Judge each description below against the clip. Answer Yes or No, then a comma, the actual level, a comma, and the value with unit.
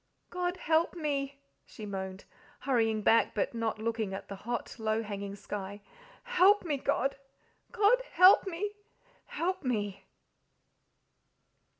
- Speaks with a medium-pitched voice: No, high, 240 Hz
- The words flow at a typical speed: No, slow, 120 wpm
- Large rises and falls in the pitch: Yes, wide, 8.9 semitones